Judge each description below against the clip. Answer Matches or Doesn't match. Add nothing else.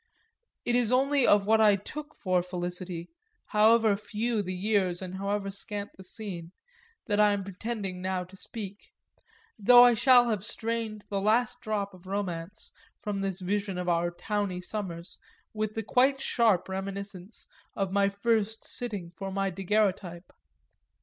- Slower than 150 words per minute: Doesn't match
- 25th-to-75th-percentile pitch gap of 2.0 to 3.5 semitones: Matches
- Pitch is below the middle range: Doesn't match